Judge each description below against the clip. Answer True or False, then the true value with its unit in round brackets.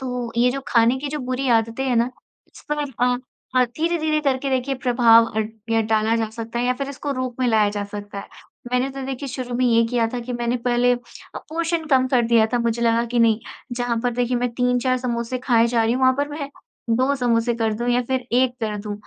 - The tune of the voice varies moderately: False (2.1 semitones)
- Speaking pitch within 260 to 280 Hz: False (245 Hz)